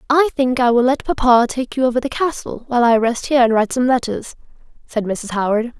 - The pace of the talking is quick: Yes, fast, 230 wpm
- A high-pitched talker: Yes, high, 245 Hz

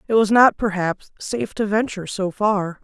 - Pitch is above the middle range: Yes, high, 205 Hz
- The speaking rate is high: No, average, 190 wpm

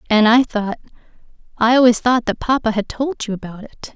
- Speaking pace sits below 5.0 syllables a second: No, 5.4 syllables/s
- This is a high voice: Yes, high, 230 Hz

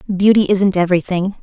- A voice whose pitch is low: No, high, 190 Hz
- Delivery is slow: Yes, slow, 125 wpm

